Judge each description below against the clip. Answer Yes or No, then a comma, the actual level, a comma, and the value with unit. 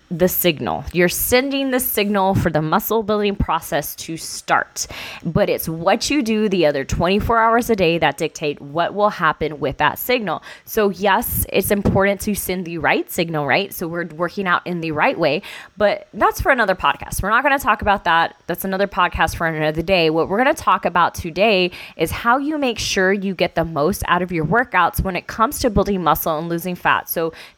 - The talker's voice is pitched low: No, medium, 185 Hz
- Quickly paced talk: Yes, fast, 215 wpm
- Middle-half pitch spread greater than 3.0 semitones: Yes, average, 4.3 semitones